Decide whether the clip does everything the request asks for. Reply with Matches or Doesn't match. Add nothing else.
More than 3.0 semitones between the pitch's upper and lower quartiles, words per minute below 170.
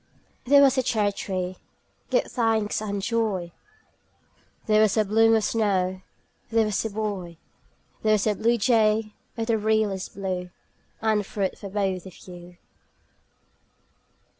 Doesn't match